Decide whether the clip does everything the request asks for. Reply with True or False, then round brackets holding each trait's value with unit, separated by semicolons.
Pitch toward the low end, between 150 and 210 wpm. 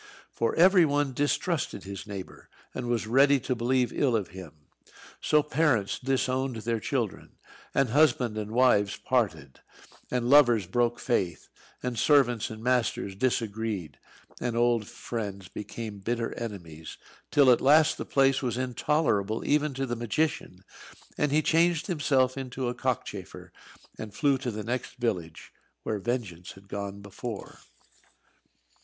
False (120 Hz; 140 wpm)